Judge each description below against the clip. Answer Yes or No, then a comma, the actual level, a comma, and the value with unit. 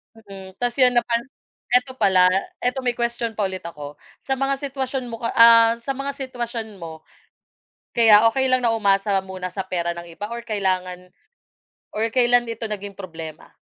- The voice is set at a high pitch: Yes, high, 225 Hz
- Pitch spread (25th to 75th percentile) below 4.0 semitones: No, average, 4.5 semitones